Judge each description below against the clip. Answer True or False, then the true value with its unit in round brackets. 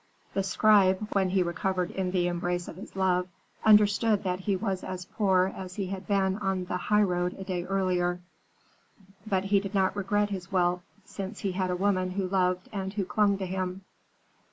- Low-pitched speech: False (190 Hz)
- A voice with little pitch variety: True (1.5 semitones)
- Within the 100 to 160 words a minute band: False (190 wpm)